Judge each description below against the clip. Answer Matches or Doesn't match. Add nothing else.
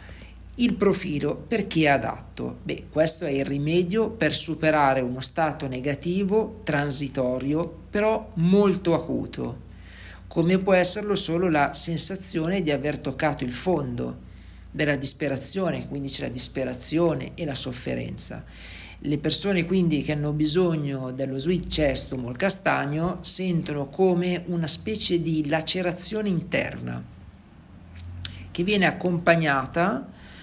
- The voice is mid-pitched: Matches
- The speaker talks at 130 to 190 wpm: Doesn't match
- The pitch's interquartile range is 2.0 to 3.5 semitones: Doesn't match